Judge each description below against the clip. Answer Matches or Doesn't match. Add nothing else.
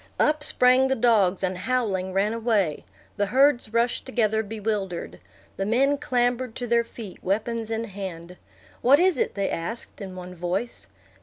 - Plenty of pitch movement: Doesn't match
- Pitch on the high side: Matches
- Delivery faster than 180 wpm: Doesn't match